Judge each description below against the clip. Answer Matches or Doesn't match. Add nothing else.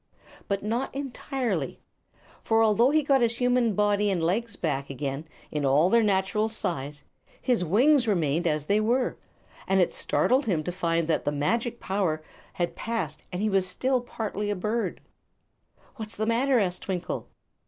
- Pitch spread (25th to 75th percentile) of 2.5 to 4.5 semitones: Doesn't match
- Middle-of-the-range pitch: Doesn't match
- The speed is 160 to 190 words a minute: Matches